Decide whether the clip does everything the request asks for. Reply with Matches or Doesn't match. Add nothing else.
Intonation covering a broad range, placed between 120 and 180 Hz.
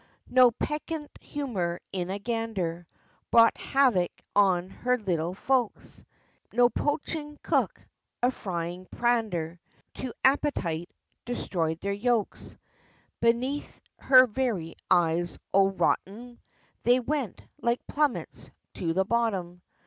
Doesn't match